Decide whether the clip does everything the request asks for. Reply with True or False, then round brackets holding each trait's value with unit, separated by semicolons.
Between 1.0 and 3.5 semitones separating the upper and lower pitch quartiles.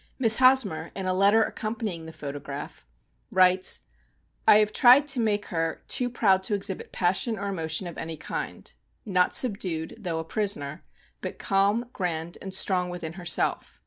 False (4.2 semitones)